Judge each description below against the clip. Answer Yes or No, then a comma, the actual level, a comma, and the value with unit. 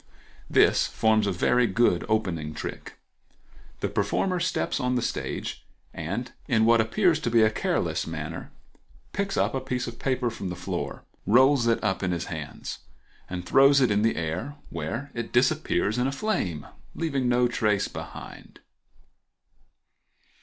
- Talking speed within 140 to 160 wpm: Yes, average, 155 wpm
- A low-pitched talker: Yes, low, 115 Hz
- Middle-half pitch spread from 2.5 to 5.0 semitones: No, wide, 5.4 semitones